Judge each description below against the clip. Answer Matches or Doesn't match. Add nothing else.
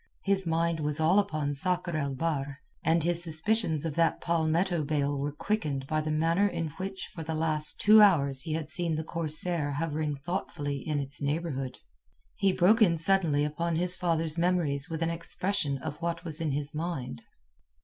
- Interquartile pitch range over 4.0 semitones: Doesn't match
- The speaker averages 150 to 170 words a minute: Doesn't match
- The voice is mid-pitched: Matches